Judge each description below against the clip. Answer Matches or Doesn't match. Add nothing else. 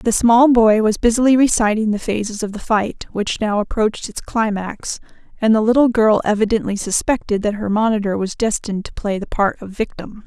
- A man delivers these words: Doesn't match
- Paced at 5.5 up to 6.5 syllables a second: Doesn't match